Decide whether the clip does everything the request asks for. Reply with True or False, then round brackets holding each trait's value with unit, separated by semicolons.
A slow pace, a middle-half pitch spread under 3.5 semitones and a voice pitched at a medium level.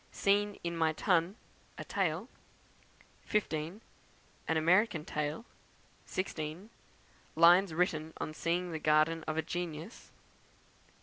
True (115 wpm; 3.1 semitones; 170 Hz)